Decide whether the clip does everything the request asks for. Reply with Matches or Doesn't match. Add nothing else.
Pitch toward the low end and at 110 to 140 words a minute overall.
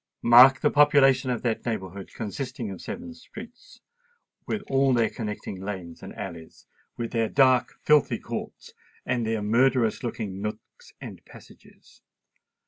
Matches